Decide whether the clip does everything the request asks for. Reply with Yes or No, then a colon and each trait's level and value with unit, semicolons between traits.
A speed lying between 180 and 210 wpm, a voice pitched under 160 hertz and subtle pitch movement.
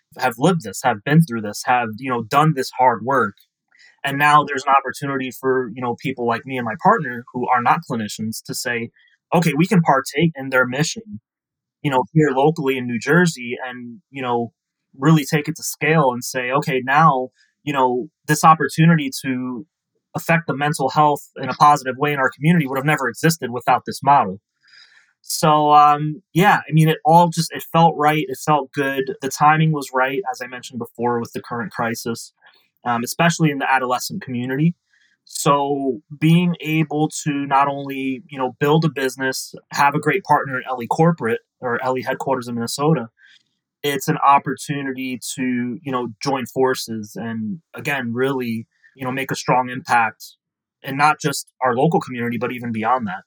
No: average, 185 wpm; low, 135 Hz; average, 3.4 semitones